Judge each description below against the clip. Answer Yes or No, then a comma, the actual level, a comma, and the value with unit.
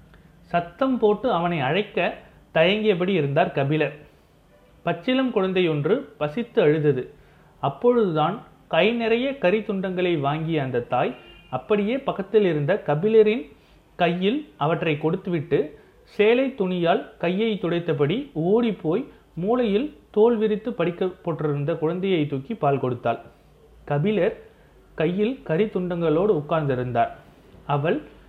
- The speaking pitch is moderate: Yes, medium, 175 Hz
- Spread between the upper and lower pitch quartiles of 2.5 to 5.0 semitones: No, wide, 5.6 semitones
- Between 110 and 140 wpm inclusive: No, average, 95 wpm